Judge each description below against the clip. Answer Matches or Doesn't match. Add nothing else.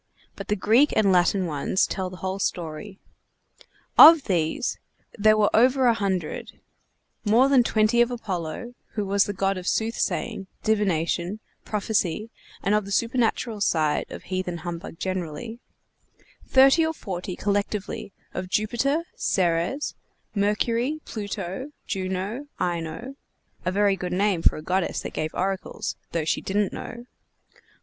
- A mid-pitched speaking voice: Doesn't match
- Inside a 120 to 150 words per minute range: Matches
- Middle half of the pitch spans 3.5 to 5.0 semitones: Matches